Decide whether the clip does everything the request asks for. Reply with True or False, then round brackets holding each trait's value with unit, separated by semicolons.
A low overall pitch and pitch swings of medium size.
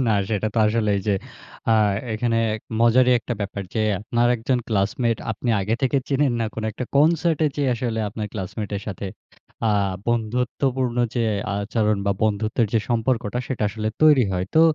True (115 Hz; 3.0 semitones)